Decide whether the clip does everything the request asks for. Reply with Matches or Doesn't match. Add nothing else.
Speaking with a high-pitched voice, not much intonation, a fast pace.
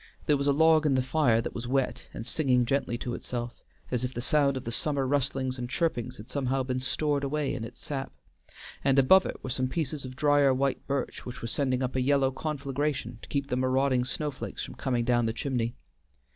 Doesn't match